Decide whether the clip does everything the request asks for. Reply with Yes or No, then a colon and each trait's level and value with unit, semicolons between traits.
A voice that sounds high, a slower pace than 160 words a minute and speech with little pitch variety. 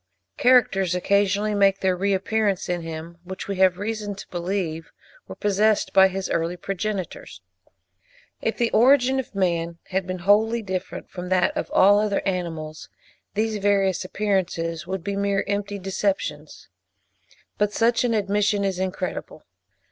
Yes: high, 195 Hz; average, 150 wpm; narrow, 2.2 semitones